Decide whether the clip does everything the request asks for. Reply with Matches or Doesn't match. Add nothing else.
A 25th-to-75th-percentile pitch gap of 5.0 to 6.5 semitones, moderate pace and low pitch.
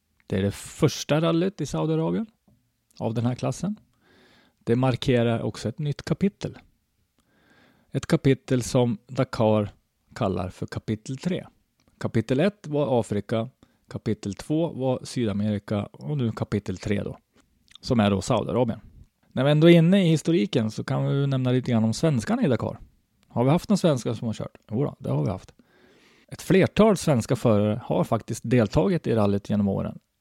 Matches